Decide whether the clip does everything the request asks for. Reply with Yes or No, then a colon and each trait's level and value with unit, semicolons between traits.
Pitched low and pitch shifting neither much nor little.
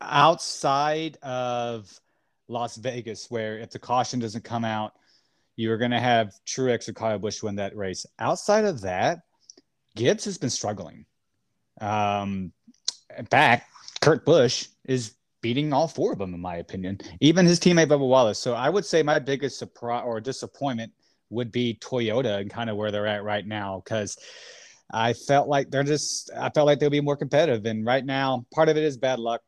Yes: low, 120 Hz; average, 4.1 semitones